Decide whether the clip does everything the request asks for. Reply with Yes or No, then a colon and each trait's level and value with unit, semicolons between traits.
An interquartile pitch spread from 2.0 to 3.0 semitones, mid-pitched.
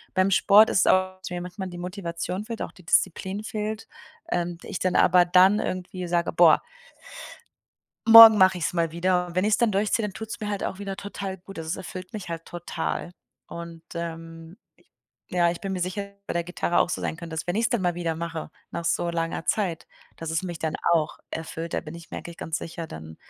Yes: narrow, 2.6 semitones; medium, 180 Hz